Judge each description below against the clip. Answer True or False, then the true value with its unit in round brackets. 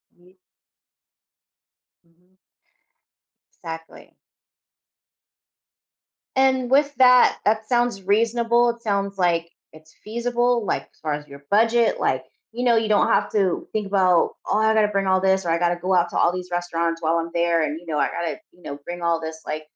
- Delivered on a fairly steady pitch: False (5.0 semitones)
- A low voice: False (185 Hz)